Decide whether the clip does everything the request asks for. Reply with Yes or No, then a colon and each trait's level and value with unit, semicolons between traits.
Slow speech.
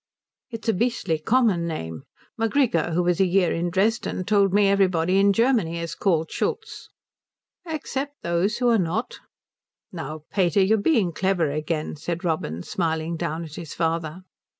No: average, 155 wpm